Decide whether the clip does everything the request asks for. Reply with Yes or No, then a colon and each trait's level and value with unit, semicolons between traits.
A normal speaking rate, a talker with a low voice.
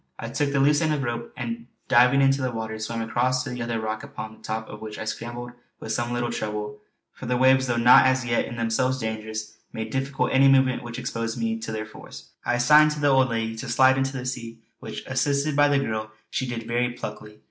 No: fast, 240 wpm; low, 120 Hz